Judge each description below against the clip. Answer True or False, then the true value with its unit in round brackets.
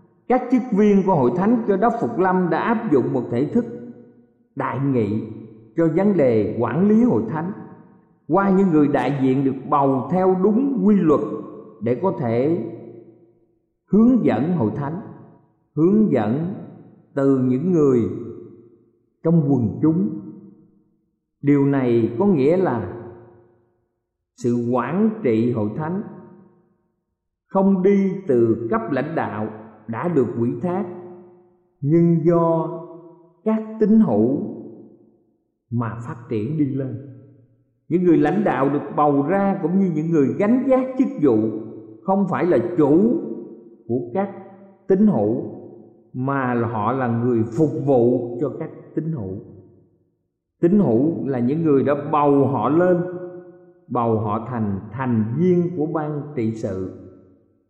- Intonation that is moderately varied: False (7.6 semitones)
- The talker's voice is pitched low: False (150 Hz)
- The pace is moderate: False (135 wpm)